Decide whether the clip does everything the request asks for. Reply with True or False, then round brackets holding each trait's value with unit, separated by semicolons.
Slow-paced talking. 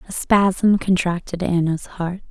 True (130 wpm)